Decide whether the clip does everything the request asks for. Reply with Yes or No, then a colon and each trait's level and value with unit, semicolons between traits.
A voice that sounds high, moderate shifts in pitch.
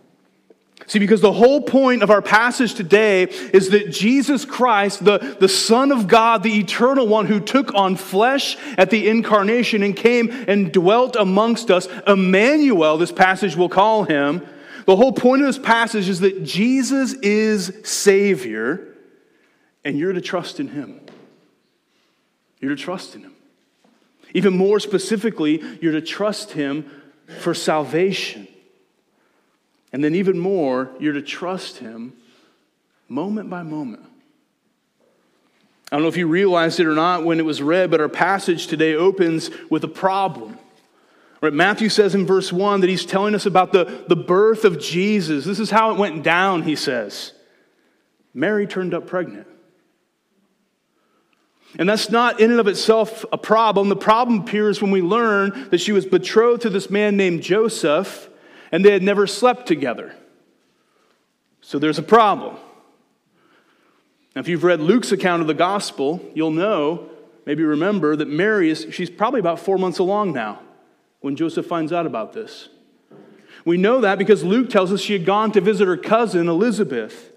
Yes: high, 200 Hz; average, 4.1 semitones